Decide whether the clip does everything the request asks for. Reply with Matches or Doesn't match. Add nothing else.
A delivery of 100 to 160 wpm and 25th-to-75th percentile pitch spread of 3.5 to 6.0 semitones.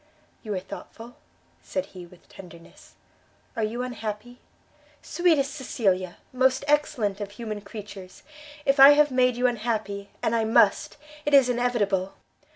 Matches